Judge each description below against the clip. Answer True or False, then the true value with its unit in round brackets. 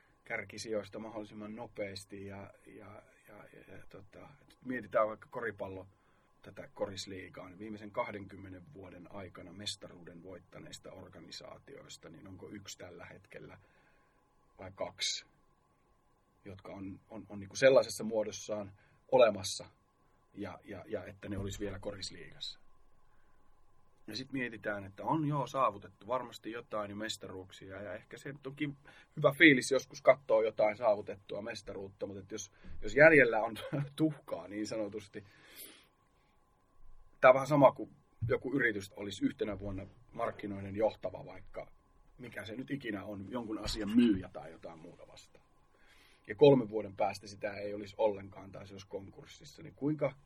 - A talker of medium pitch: False (105 Hz)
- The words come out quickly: False (140 wpm)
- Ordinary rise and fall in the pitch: True (3.6 semitones)